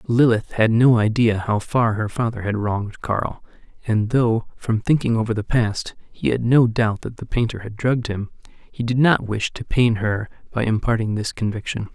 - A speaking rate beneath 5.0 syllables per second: Yes, 4.8 syllables/s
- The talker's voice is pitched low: Yes, low, 115 Hz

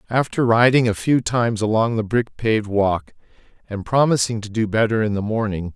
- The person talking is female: No, male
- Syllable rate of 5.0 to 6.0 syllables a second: Yes, 5.4 syllables/s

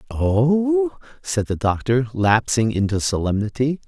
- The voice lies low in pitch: Yes, low, 130 Hz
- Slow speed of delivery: Yes, slow, 110 wpm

